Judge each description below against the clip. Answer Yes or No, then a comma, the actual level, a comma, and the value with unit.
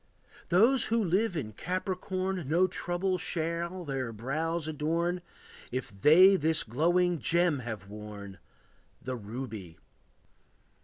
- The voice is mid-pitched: Yes, medium, 165 Hz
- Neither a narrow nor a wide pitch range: No, wide, 6.4 semitones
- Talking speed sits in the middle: No, slow, 110 wpm